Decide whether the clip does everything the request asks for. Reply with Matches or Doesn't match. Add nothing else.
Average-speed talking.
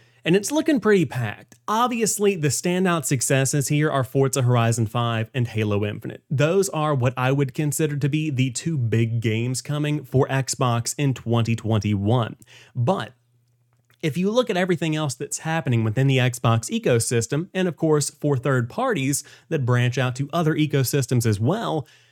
Matches